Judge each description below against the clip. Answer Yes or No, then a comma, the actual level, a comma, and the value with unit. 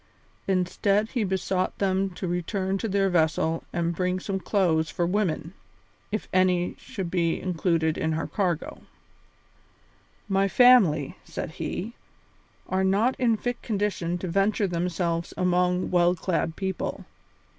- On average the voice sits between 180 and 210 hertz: Yes, medium, 185 Hz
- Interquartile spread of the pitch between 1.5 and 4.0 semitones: Yes, narrow, 2.4 semitones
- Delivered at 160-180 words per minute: No, average, 140 wpm